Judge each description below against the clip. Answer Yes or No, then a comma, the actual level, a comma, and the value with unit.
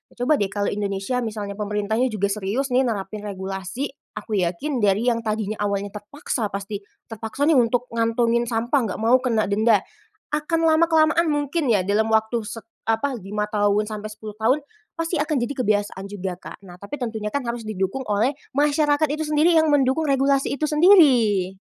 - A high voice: Yes, high, 225 Hz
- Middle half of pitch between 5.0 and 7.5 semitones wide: Yes, average, 5.3 semitones